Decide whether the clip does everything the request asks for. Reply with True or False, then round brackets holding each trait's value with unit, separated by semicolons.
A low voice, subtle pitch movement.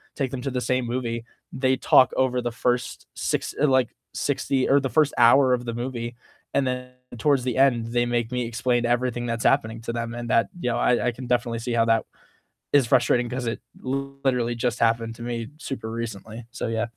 True (120 Hz; 1.8 semitones)